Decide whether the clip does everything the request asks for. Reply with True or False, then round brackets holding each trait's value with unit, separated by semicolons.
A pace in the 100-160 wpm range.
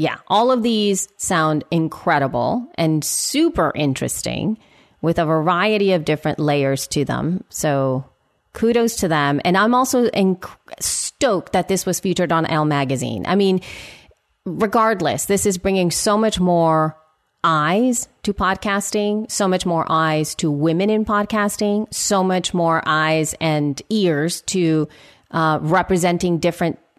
True (140 wpm)